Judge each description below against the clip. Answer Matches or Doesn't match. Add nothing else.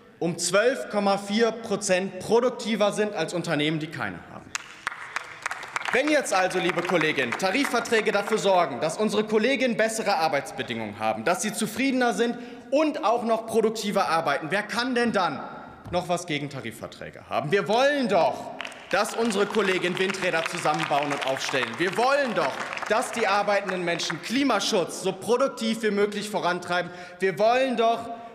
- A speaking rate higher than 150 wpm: Doesn't match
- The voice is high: Matches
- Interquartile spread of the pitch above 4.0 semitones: Matches